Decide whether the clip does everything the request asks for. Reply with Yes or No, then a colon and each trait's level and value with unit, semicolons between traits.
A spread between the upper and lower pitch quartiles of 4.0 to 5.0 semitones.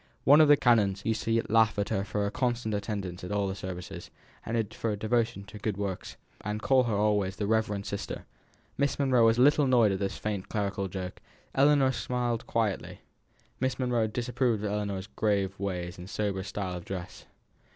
No: average, 3.2 semitones